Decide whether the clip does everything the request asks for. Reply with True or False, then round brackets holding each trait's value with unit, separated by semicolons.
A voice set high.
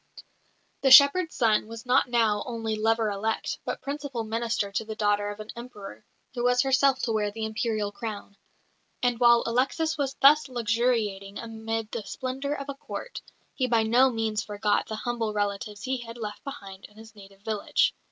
True (225 Hz)